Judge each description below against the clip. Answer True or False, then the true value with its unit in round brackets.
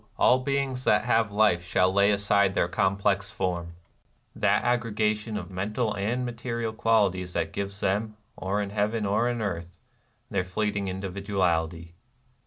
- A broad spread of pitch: False (2.9 semitones)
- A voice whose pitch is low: True (100 Hz)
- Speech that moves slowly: False (150 wpm)